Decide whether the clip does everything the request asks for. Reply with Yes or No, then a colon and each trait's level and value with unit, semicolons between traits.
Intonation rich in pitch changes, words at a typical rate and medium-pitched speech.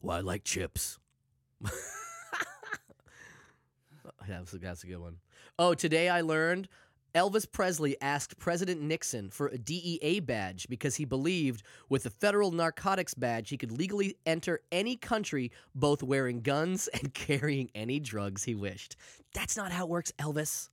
Yes: wide, 5.9 semitones; average, 150 wpm; medium, 150 Hz